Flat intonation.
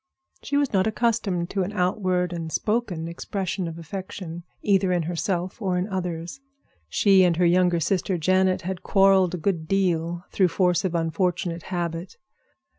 Yes: narrow, 2.1 semitones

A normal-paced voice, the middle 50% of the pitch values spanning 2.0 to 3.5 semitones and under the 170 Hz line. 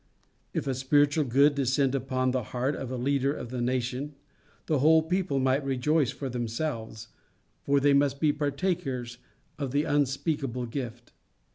Yes: average, 155 wpm; narrow, 2.5 semitones; low, 135 Hz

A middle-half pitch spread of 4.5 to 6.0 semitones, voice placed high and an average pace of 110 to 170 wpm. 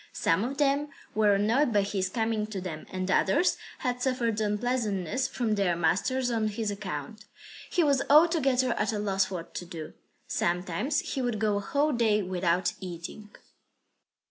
Yes: average, 4.9 semitones; high, 210 Hz; average, 165 wpm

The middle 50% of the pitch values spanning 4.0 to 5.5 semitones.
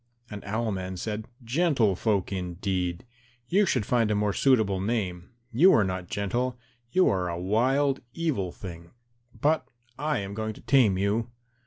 Yes: average, 5.1 semitones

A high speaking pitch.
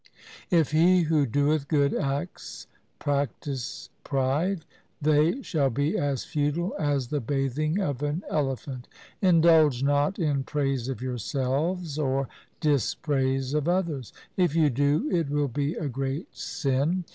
No: medium, 145 Hz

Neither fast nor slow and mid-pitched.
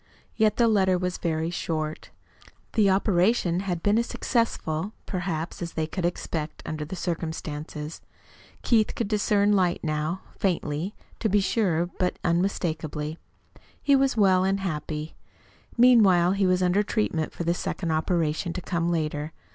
Yes: average, 145 wpm; medium, 175 Hz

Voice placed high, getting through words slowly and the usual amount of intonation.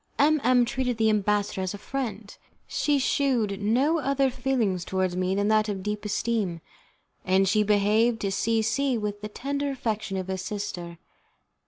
No: high, 215 Hz; average, 170 wpm; average, 4.2 semitones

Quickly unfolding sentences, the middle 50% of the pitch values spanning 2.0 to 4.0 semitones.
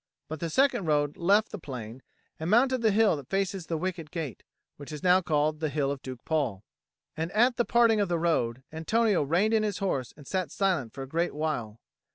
No: fast, 215 wpm; wide, 5.5 semitones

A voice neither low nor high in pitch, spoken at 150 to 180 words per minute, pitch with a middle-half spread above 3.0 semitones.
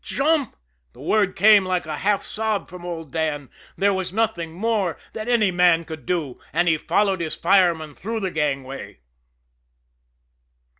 Yes: medium, 180 Hz; average, 155 wpm; average, 4.5 semitones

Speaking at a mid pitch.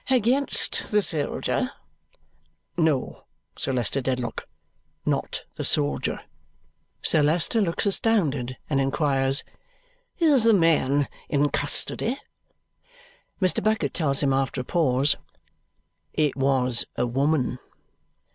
Yes: medium, 145 Hz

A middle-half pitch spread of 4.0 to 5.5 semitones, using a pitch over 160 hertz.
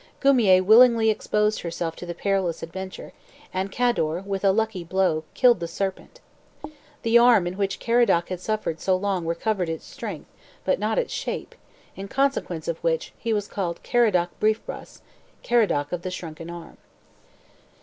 Yes: average, 4.4 semitones; high, 190 Hz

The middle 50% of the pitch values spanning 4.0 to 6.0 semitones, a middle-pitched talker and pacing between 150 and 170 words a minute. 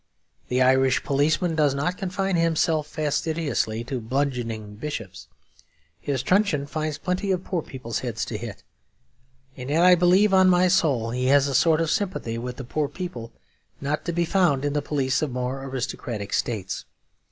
Yes: average, 5.1 semitones; medium, 145 Hz; average, 165 wpm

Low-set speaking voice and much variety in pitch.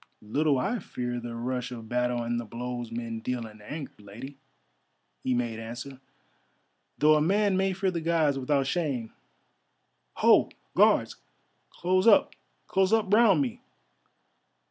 Yes: low, 130 Hz; wide, 6.0 semitones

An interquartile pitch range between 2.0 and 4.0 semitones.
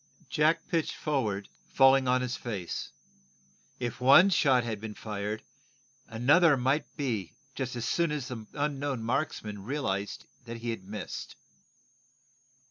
No: average, 4.7 semitones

